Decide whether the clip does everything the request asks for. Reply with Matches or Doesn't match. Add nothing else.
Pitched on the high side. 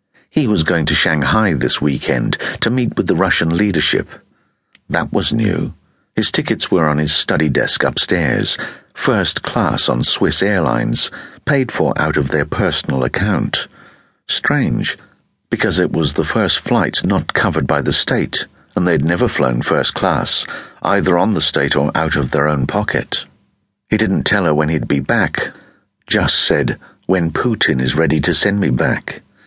Doesn't match